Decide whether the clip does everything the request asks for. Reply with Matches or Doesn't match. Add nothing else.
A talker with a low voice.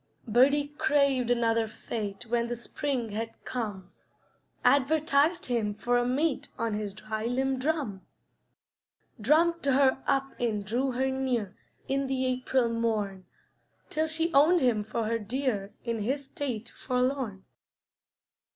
Doesn't match